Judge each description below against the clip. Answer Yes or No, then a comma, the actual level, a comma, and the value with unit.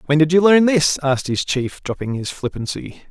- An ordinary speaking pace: No, fast, 210 wpm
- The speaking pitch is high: No, medium, 150 Hz